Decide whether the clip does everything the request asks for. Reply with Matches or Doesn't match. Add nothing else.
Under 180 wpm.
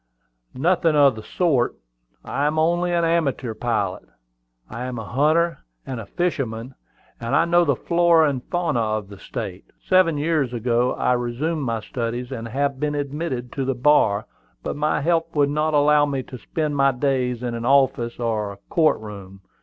Doesn't match